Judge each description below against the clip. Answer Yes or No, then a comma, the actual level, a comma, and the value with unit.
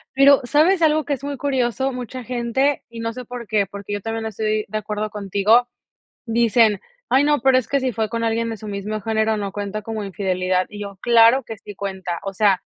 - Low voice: No, high, 225 Hz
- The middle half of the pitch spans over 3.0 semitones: Yes, average, 3.5 semitones